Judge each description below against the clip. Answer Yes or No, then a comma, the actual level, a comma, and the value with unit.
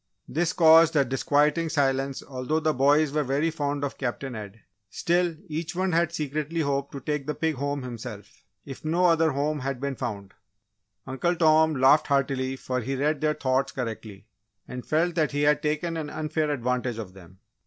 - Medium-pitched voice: Yes, medium, 145 Hz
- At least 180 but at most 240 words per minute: Yes, average, 185 wpm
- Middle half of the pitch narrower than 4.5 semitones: Yes, average, 3.2 semitones